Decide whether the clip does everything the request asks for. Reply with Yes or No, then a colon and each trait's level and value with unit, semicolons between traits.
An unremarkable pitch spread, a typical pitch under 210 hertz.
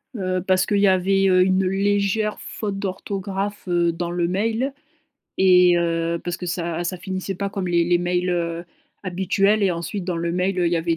No: narrow, 2.1 semitones; medium, 185 Hz